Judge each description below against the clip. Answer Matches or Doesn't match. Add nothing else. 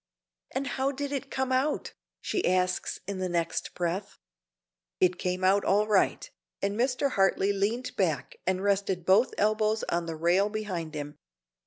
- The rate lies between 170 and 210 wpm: Doesn't match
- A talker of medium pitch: Doesn't match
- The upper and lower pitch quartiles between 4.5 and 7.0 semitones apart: Doesn't match